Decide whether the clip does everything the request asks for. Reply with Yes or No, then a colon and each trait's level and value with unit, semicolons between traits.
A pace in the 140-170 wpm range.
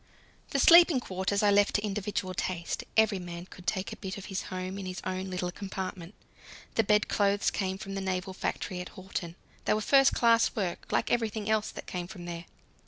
No: average, 200 wpm